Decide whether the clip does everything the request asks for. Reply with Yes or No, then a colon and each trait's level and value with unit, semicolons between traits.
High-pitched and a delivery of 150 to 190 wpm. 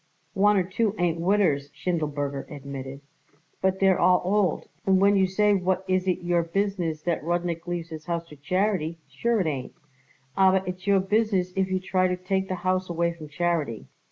No: medium, 180 Hz; average, 185 wpm